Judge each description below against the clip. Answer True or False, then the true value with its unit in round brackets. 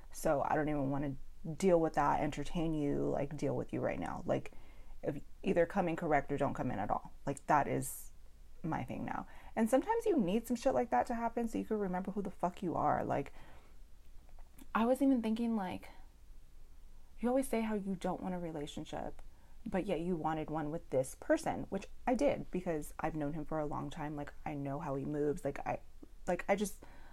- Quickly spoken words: True (220 wpm)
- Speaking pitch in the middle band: True (155 Hz)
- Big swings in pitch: True (6.4 semitones)